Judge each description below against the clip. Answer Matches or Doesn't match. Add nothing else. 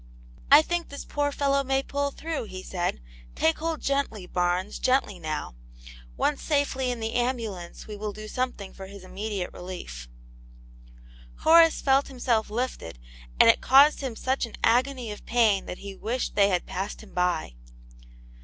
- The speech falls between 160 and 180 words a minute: Matches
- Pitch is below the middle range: Doesn't match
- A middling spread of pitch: Doesn't match